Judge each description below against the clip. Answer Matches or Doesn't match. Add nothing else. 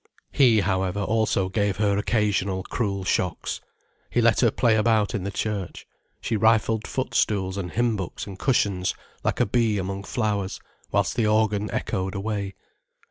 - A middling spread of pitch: Doesn't match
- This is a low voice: Matches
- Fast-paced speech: Doesn't match